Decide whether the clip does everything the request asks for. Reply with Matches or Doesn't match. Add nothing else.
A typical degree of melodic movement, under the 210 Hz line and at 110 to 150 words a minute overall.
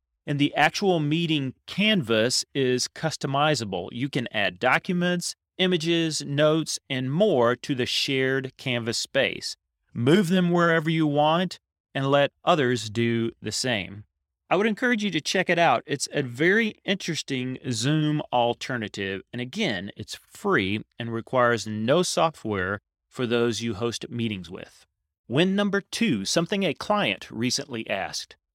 Doesn't match